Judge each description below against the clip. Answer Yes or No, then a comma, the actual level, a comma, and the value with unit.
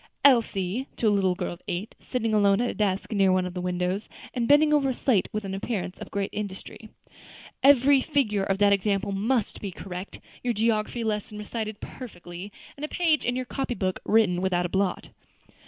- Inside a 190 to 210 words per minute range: Yes, average, 195 wpm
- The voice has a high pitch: Yes, high, 210 Hz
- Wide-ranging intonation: No, average, 4.2 semitones